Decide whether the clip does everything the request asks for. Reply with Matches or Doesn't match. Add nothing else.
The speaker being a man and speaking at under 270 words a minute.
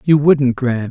Matches